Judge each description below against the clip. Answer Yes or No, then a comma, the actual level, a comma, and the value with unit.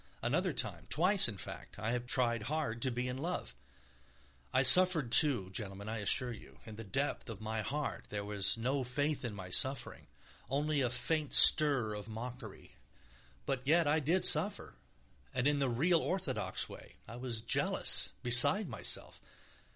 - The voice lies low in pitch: Yes, low, 125 Hz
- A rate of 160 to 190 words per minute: Yes, average, 165 wpm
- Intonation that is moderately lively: Yes, average, 4.9 semitones